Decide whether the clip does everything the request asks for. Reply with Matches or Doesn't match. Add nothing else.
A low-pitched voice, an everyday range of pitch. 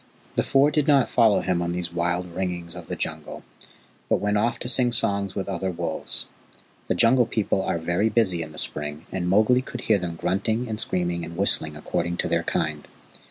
Matches